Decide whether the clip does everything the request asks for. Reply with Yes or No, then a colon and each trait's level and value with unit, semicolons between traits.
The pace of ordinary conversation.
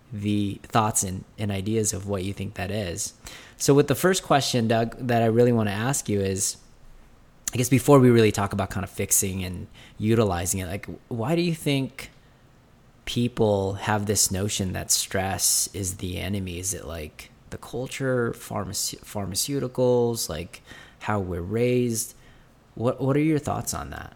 Yes: average, 175 wpm